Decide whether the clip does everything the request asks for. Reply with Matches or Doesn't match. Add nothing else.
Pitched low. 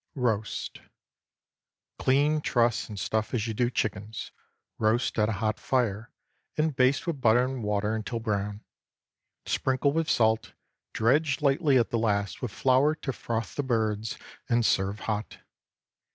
Matches